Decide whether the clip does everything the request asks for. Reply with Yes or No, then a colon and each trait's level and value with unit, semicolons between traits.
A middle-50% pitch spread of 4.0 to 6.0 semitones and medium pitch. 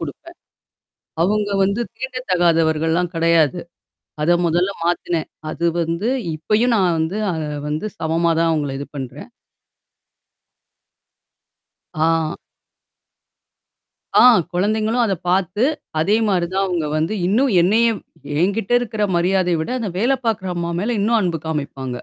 Yes: average, 4.5 semitones; medium, 175 Hz